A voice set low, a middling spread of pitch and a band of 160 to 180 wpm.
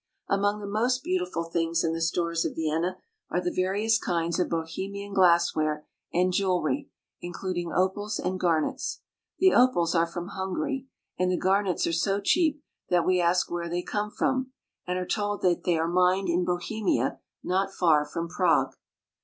No: medium, 180 Hz; average, 3.1 semitones; average, 170 wpm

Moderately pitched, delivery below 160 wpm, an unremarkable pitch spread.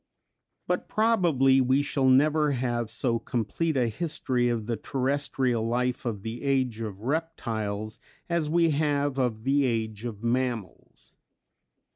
No: low, 130 Hz; slow, 135 wpm; average, 3.9 semitones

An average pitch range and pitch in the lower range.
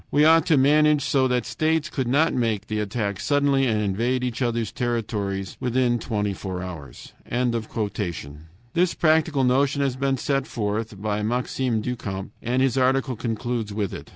Yes: average, 4.4 semitones; low, 125 Hz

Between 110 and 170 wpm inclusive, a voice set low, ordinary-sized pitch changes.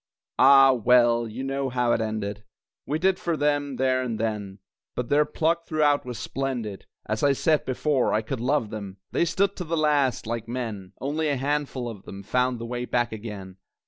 No: average, 195 wpm; low, 125 Hz; average, 4.4 semitones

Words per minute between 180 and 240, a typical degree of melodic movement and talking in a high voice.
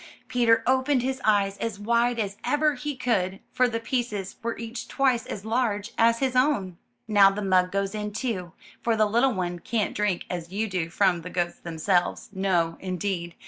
Yes: average, 185 wpm; average, 4.2 semitones; high, 210 Hz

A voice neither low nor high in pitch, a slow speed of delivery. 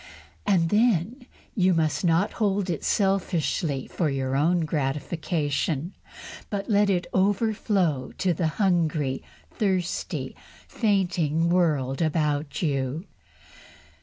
Yes: medium, 170 Hz; slow, 105 wpm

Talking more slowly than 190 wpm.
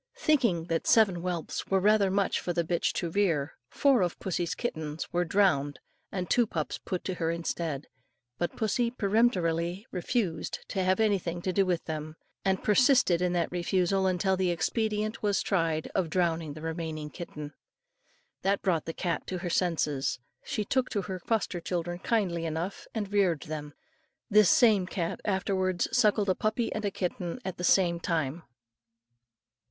Yes: average, 170 wpm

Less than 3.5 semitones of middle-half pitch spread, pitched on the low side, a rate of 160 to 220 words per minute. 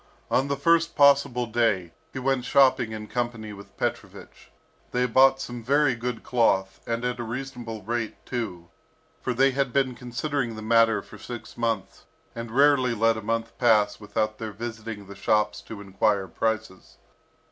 Yes: average, 2.8 semitones; low, 115 Hz; average, 165 wpm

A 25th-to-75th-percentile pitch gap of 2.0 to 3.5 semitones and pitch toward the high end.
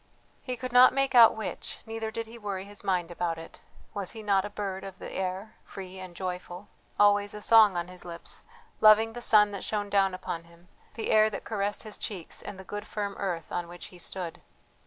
Yes: average, 2.9 semitones; high, 200 Hz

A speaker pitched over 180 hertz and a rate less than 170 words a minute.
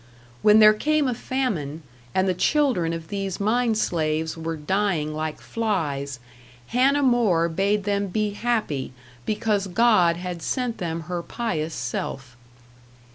Yes: high, 190 Hz; slow, 135 wpm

